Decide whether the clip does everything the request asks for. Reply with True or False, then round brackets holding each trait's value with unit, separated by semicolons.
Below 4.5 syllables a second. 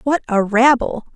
True (4.3 syllables/s)